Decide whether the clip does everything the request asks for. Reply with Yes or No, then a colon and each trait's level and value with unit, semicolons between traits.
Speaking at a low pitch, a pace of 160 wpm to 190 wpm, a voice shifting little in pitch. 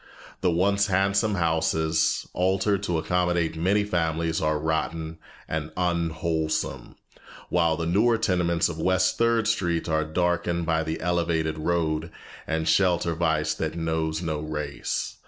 No: very low, 85 Hz; slow, 135 wpm; narrow, 2.1 semitones